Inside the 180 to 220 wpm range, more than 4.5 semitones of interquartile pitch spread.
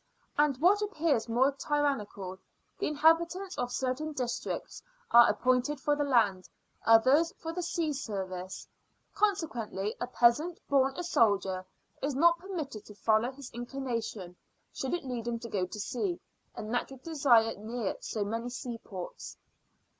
No: average, 145 wpm; average, 5.1 semitones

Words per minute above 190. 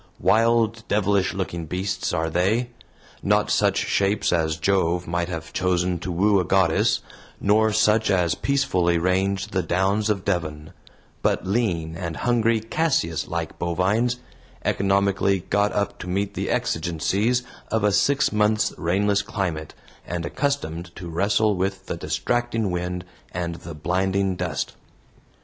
No: average, 140 wpm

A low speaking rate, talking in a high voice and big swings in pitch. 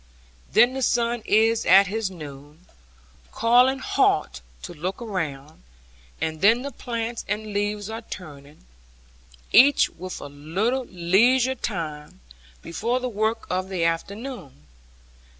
Yes: slow, 125 wpm; high, 205 Hz; wide, 6.0 semitones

